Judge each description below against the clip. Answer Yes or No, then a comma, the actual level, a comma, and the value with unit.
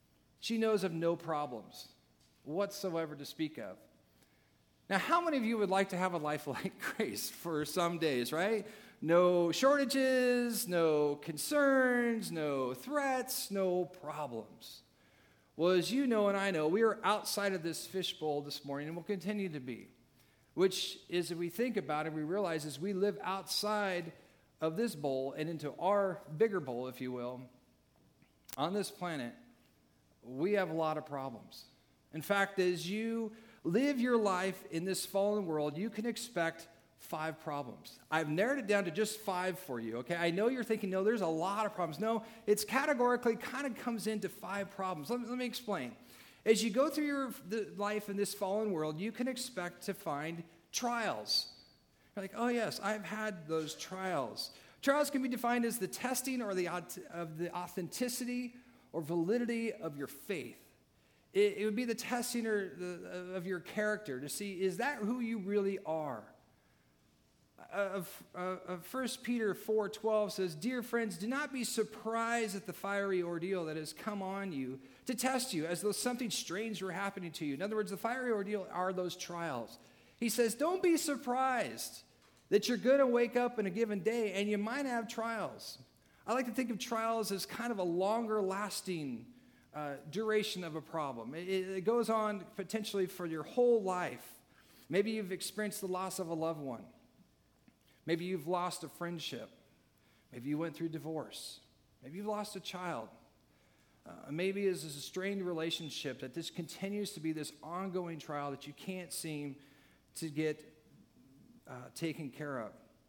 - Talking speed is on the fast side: No, average, 175 wpm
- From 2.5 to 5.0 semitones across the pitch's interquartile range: No, wide, 5.5 semitones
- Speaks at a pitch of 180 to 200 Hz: Yes, high, 190 Hz